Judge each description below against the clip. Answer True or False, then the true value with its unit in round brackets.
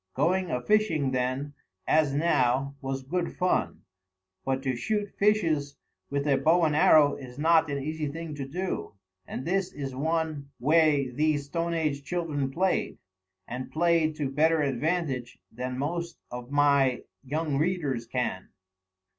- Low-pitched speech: False (145 Hz)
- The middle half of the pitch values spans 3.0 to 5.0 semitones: True (3.5 semitones)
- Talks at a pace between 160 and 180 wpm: False (145 wpm)